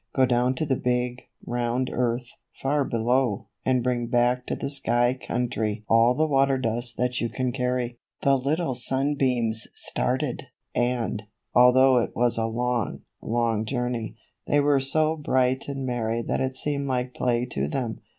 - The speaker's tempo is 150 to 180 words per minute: Yes, average, 160 wpm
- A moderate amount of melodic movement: No, narrow, 1.9 semitones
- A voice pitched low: Yes, low, 125 Hz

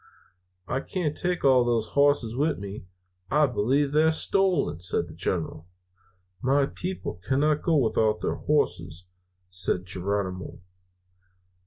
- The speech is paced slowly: Yes, slow, 125 wpm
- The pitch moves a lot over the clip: Yes, wide, 7.2 semitones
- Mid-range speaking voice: No, low, 130 Hz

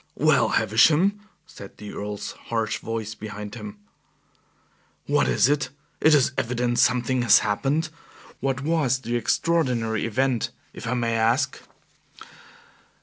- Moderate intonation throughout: Yes, average, 3.4 semitones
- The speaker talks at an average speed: No, slow, 125 wpm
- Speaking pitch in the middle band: No, low, 120 Hz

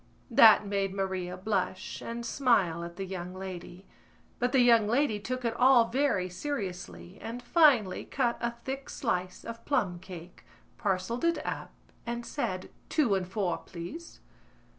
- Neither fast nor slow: Yes, average, 145 wpm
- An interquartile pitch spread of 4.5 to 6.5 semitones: Yes, average, 4.9 semitones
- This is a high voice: Yes, high, 210 Hz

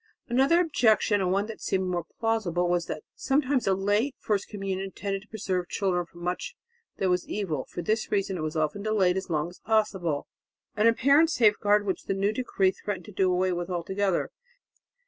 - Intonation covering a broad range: No, average, 3.1 semitones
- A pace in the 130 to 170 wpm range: No, average, 190 wpm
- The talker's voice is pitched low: No, high, 195 Hz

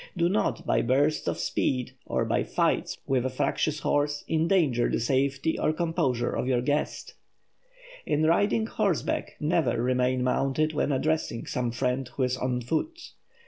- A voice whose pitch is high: No, medium, 140 Hz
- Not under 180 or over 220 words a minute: No, average, 155 wpm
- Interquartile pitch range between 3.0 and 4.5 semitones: Yes, average, 3.8 semitones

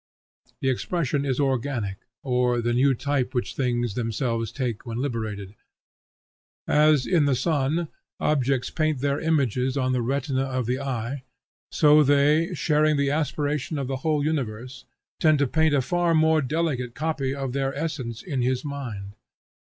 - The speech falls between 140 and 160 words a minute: Yes, average, 155 wpm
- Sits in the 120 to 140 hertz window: Yes, low, 135 Hz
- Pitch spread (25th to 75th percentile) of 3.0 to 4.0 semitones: Yes, average, 3.3 semitones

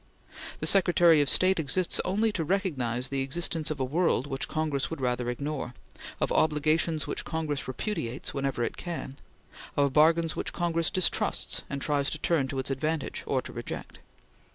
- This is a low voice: No, medium, 150 Hz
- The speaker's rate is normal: Yes, average, 170 wpm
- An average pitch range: Yes, average, 3.8 semitones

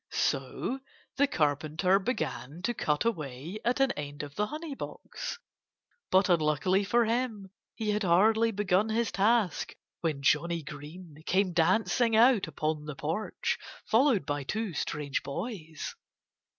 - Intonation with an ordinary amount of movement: No, wide, 6.6 semitones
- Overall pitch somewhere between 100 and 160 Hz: No, medium, 185 Hz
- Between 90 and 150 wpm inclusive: Yes, slow, 135 wpm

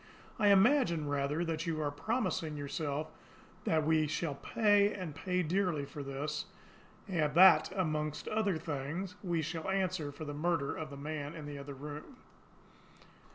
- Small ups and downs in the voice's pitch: No, average, 3.9 semitones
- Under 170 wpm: Yes, average, 155 wpm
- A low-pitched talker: No, medium, 155 Hz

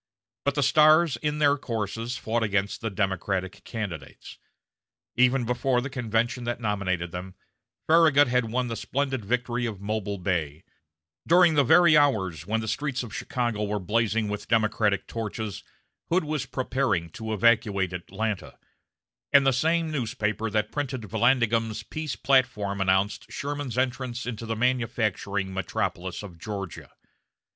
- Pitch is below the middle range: Yes, low, 115 Hz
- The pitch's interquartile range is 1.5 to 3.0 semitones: No, average, 4.3 semitones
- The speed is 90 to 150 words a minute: Yes, average, 140 wpm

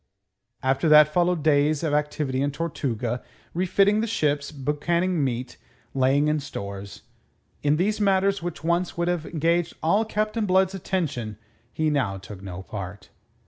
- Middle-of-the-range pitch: Yes, medium, 150 Hz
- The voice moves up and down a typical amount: Yes, average, 5.0 semitones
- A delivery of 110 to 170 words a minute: Yes, average, 145 wpm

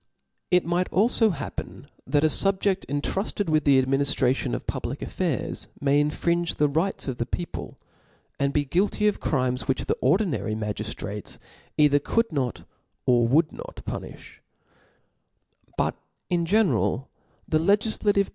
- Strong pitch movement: Yes, wide, 6.0 semitones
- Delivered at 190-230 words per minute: No, slow, 135 wpm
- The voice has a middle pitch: Yes, medium, 150 Hz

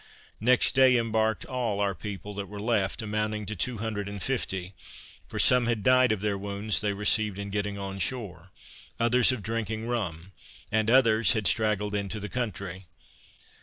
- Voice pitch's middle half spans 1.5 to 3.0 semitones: Yes, narrow, 2.4 semitones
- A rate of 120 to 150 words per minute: No, average, 170 wpm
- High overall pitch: No, low, 105 Hz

